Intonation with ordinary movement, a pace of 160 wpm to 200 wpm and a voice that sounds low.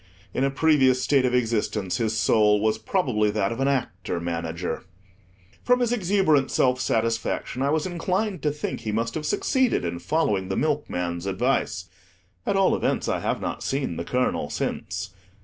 No: wide, 6.6 semitones; average, 170 wpm; low, 125 Hz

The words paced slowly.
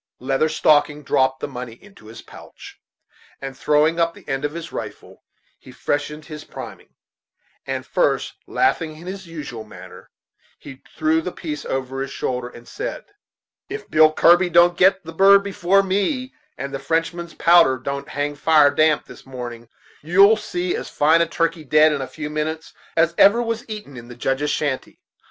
No: average, 175 wpm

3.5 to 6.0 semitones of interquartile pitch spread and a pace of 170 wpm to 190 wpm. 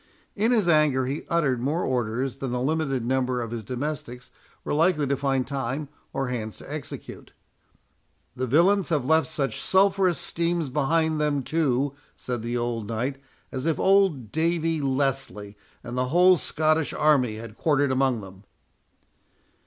No: average, 4.2 semitones; average, 155 wpm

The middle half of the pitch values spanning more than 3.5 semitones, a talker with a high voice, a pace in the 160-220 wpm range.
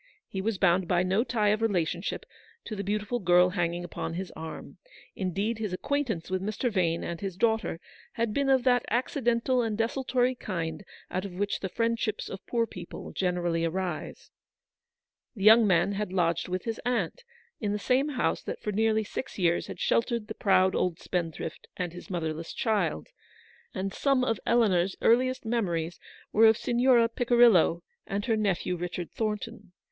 Yes: average, 4.4 semitones; high, 205 Hz; average, 175 wpm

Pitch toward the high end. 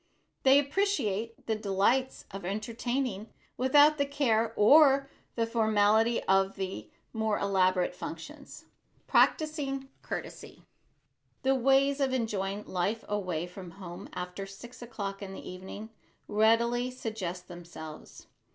Yes: high, 220 Hz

